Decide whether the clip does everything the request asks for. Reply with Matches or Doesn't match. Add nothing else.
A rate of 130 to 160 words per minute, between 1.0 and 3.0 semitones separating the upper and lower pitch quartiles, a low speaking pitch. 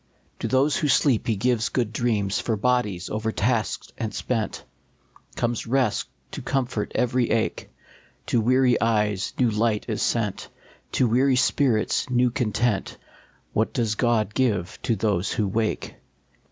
Matches